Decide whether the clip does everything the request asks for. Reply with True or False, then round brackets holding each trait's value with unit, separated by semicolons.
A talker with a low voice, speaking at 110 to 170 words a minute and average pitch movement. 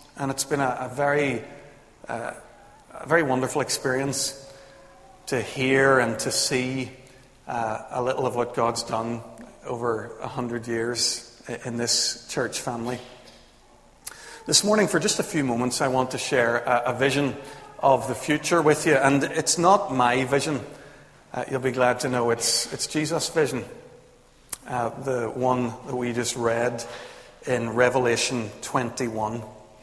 False (125 Hz; 150 wpm; 2.3 semitones)